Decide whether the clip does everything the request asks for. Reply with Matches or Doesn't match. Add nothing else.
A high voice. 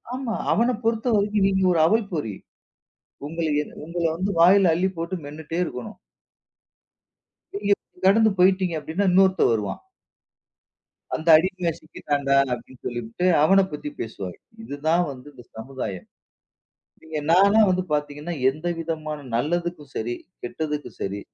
Doesn't match